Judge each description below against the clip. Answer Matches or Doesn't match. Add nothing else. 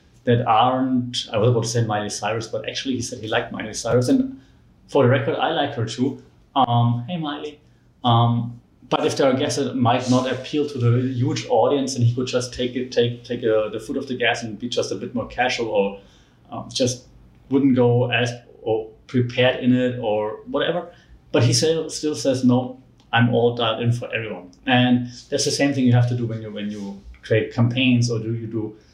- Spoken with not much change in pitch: Matches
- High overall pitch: Doesn't match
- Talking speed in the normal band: Doesn't match